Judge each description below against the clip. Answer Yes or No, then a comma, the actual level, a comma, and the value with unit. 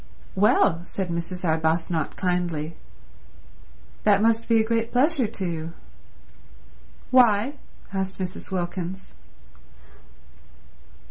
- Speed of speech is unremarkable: No, slow, 90 wpm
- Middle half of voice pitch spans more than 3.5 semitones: Yes, average, 4.6 semitones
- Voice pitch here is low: No, medium, 185 Hz